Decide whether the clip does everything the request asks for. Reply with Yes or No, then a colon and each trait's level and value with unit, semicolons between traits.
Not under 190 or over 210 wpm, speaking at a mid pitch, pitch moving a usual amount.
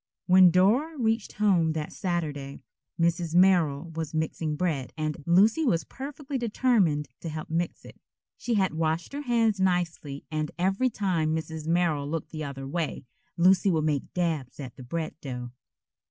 No: average, 160 wpm; medium, 170 Hz; average, 3.8 semitones